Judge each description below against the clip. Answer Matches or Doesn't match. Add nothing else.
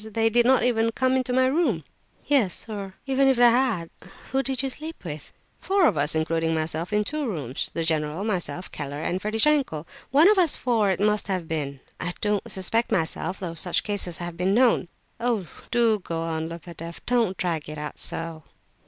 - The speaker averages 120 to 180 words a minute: Doesn't match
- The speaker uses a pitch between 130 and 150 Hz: Doesn't match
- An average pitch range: Doesn't match